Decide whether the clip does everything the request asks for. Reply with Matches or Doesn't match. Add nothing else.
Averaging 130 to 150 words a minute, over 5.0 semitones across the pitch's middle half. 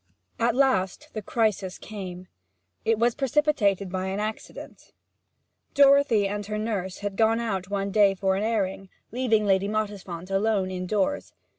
Doesn't match